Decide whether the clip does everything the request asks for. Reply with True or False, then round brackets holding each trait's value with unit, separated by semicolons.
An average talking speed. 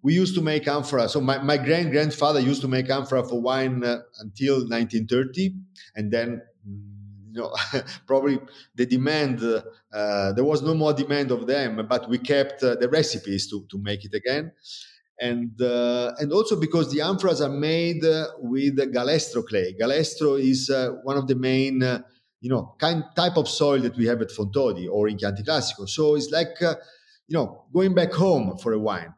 True (190 wpm)